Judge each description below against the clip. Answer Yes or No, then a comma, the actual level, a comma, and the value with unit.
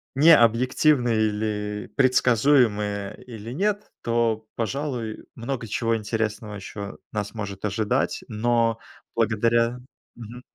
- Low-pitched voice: Yes, low, 115 Hz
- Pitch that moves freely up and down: No, narrow, 2.6 semitones